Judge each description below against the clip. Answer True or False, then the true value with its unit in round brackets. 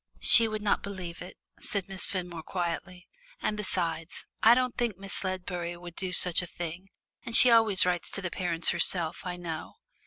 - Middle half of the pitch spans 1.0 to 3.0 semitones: True (2.5 semitones)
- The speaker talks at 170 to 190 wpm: True (185 wpm)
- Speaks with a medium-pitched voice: True (180 Hz)